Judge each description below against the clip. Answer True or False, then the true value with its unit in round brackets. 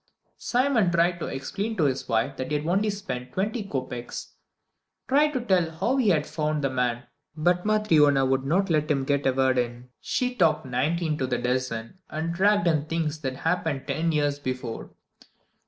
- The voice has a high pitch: False (155 Hz)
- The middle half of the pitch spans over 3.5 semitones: True (5.6 semitones)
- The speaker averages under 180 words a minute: False (190 wpm)